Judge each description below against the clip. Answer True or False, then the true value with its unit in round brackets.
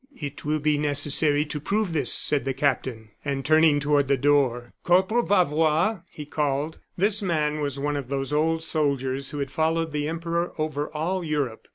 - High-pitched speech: False (150 Hz)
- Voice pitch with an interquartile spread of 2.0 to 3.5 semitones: True (2.4 semitones)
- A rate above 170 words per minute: True (180 wpm)